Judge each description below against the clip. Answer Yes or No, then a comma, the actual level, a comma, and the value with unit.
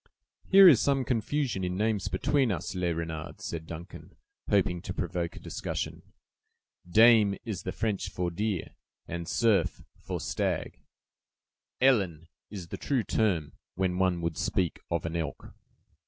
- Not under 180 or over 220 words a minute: No, average, 145 wpm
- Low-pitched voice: Yes, very low, 95 Hz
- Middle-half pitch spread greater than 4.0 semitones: Yes, average, 4.8 semitones